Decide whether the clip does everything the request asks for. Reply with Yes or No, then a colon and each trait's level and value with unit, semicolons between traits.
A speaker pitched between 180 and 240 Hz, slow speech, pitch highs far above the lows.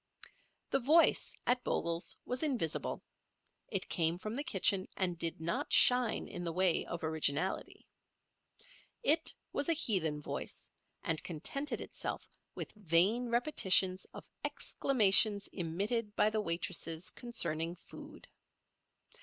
Yes: high, 190 Hz; slow, 120 wpm; wide, 6.3 semitones